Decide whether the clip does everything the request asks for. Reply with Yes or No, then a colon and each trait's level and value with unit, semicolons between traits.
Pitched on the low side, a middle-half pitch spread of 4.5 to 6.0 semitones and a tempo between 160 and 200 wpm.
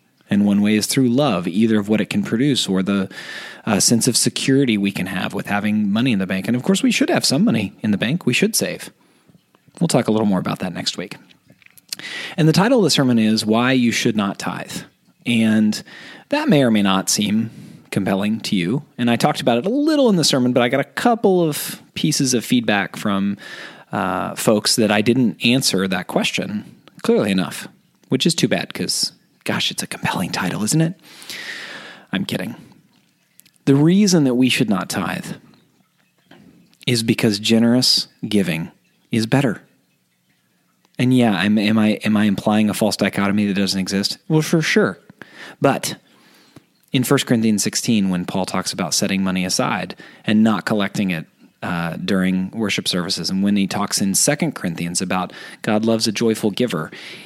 Yes: low, 115 Hz; average, 5.3 semitones; average, 190 wpm